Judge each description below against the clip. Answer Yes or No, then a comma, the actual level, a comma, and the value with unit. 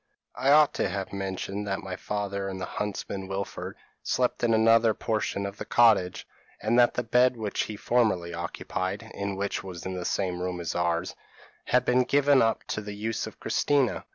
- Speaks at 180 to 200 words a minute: Yes, average, 190 wpm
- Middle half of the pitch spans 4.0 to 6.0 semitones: No, average, 3.6 semitones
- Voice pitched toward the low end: Yes, low, 105 Hz